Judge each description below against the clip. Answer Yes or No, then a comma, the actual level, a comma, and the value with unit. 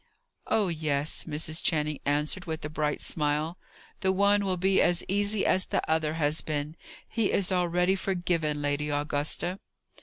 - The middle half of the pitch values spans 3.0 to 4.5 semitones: Yes, average, 3.8 semitones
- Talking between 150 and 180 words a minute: Yes, average, 155 wpm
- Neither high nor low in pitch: Yes, medium, 160 Hz